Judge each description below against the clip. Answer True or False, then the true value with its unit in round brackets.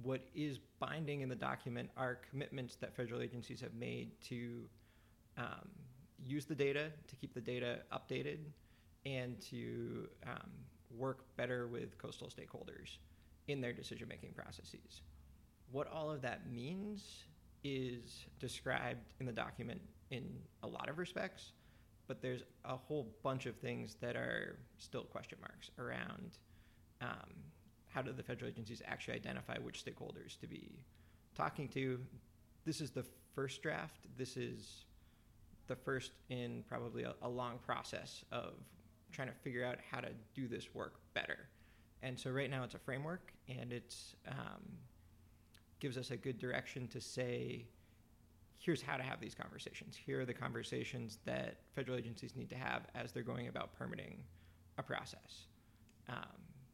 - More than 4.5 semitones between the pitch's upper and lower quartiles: False (3.8 semitones)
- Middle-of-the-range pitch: False (125 Hz)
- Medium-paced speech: True (155 wpm)